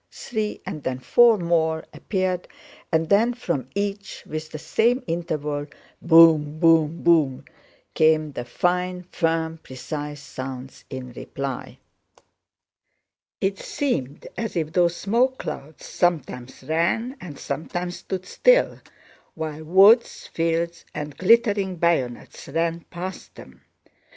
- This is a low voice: No, medium, 165 Hz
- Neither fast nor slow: No, slow, 110 wpm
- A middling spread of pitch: Yes, average, 4.0 semitones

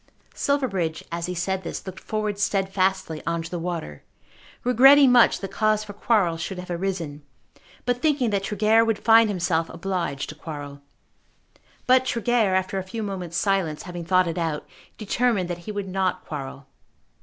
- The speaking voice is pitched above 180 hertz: Yes, high, 190 Hz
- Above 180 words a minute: No, average, 165 wpm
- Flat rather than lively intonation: No, average, 4.1 semitones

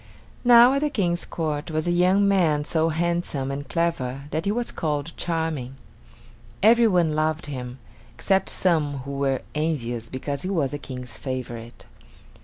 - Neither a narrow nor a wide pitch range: Yes, average, 4.3 semitones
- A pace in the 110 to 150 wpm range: No, average, 160 wpm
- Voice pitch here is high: No, medium, 155 Hz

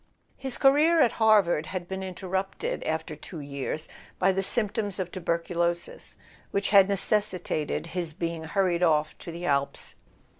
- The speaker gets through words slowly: No, average, 145 wpm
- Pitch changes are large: No, average, 3.1 semitones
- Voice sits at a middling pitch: Yes, medium, 180 Hz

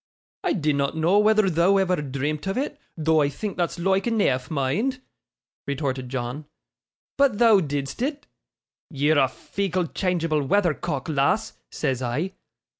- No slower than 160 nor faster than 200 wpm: No, average, 140 wpm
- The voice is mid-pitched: Yes, medium, 160 Hz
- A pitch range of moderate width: No, wide, 5.8 semitones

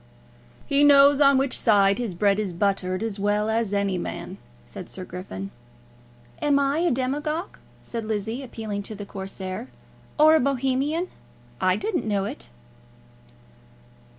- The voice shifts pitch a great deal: Yes, wide, 5.9 semitones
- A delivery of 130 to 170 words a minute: Yes, average, 145 wpm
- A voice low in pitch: No, high, 220 Hz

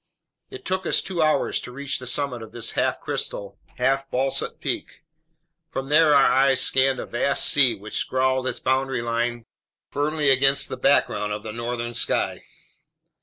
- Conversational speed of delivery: Yes, average, 170 wpm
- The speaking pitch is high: No, low, 130 Hz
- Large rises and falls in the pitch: No, average, 2.8 semitones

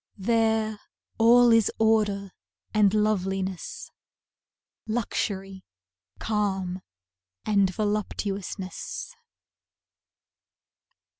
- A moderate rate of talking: No, slow, 55 wpm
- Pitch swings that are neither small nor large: No, narrow, 2.3 semitones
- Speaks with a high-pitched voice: Yes, high, 210 Hz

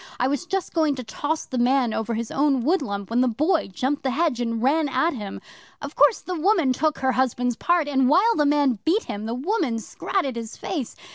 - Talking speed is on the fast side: Yes, fast, 220 wpm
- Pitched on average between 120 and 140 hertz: No, very high, 270 Hz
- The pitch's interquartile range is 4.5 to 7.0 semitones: Yes, average, 4.9 semitones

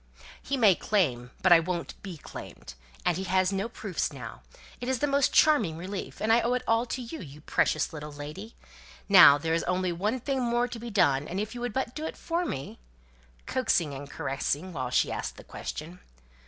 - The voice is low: No, high, 190 Hz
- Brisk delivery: Yes, fast, 210 wpm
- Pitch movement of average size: No, wide, 7.4 semitones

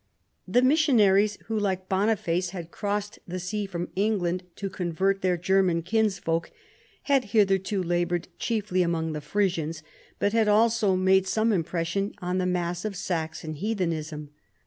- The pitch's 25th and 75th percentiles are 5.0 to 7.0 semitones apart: No, average, 3.2 semitones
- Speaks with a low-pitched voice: No, high, 190 Hz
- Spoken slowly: No, average, 145 wpm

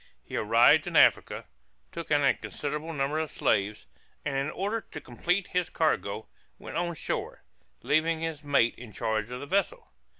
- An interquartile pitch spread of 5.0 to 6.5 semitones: Yes, wide, 5.5 semitones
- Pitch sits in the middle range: Yes, medium, 150 Hz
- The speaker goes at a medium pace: Yes, average, 170 wpm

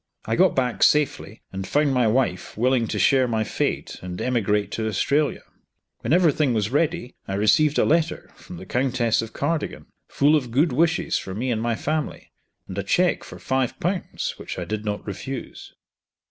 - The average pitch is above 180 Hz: No, low, 125 Hz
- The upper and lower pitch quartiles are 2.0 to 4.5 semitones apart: No, wide, 5.4 semitones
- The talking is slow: No, average, 190 wpm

